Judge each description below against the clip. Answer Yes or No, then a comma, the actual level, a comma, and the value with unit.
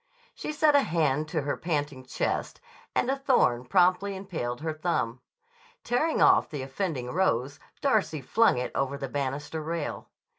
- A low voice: No, medium, 155 Hz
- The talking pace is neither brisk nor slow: Yes, average, 155 wpm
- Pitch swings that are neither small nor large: No, wide, 6.2 semitones